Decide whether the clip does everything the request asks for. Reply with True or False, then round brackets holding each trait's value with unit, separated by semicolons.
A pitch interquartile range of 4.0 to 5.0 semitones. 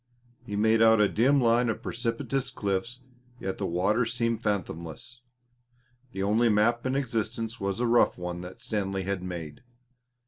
False (3.5 semitones)